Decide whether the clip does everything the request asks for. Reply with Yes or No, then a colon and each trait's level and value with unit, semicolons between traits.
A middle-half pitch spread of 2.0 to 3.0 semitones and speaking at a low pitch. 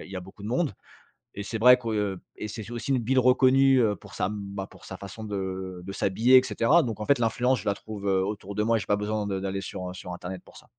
No: average, 3.7 semitones; low, 105 Hz